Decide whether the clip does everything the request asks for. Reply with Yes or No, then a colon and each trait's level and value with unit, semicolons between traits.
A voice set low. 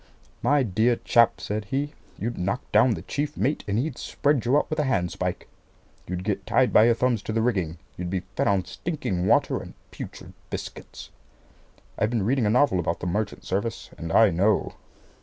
Yes: low, 110 Hz